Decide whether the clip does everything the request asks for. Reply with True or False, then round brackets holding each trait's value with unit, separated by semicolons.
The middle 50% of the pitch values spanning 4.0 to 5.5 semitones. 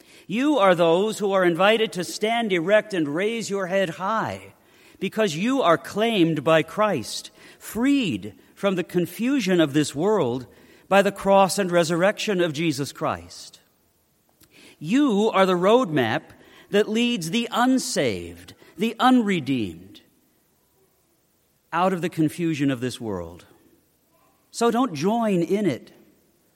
True (5.0 semitones)